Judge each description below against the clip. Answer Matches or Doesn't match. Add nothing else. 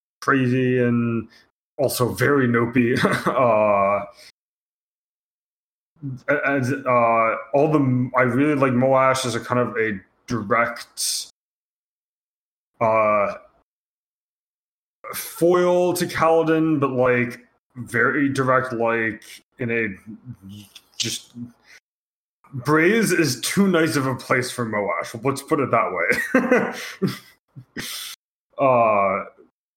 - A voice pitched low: Matches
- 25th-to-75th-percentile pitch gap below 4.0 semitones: Matches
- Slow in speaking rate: Matches